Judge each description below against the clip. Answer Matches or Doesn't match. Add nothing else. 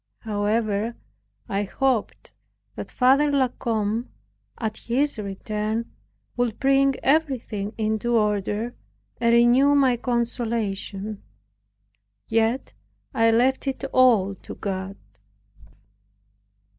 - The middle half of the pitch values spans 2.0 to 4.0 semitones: Matches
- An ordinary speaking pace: Doesn't match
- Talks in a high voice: Matches